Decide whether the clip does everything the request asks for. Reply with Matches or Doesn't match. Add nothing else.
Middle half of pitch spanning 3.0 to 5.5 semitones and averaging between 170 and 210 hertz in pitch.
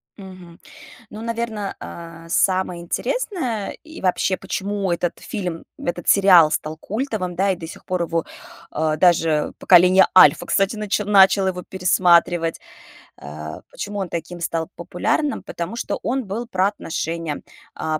Matches